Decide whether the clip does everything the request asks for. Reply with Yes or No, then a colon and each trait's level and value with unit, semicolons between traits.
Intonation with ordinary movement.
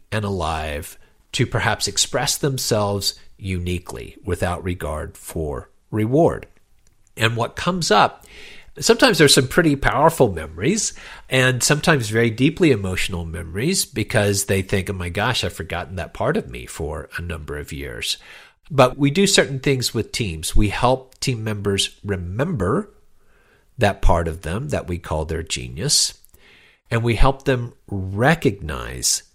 No: wide, 6.9 semitones